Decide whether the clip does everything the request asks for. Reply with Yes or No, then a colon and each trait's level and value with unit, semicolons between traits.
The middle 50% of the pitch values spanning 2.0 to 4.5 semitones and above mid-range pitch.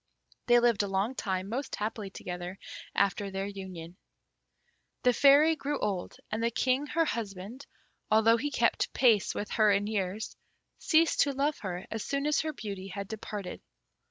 No: average, 5.0 semitones; high, 215 Hz